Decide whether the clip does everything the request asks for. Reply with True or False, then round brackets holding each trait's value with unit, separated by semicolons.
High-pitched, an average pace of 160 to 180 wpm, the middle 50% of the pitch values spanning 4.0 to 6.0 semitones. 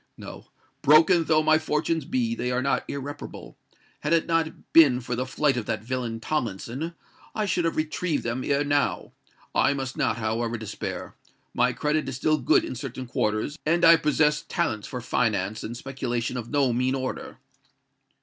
False (135 Hz; 170 wpm; 4.4 semitones)